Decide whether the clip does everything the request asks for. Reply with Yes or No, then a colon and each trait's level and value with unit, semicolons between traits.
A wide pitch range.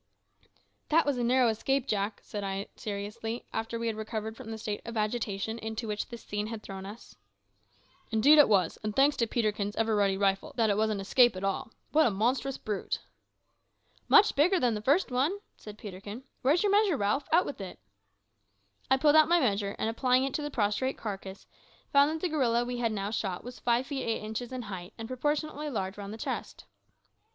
No: average, 4.3 semitones